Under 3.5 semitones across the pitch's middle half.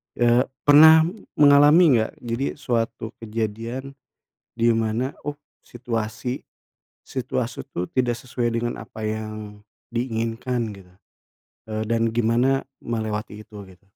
Yes: narrow, 2.6 semitones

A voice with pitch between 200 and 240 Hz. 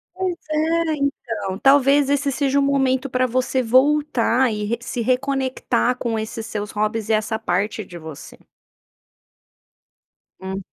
No: very high, 255 Hz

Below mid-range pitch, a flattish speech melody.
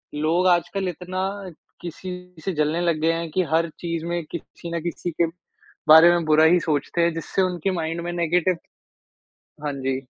No: medium, 170 Hz; narrow, 1.6 semitones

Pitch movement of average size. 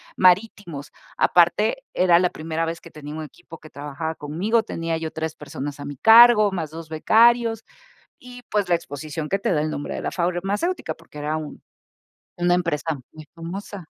Yes: average, 4.3 semitones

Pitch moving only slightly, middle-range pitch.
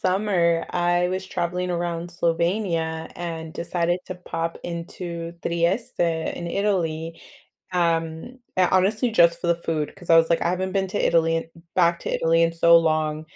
Yes: narrow, 1.6 semitones; medium, 170 Hz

